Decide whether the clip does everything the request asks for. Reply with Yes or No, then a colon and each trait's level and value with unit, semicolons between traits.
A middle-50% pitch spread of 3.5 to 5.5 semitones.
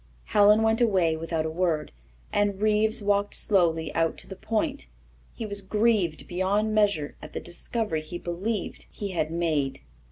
Yes: average, 4.5 semitones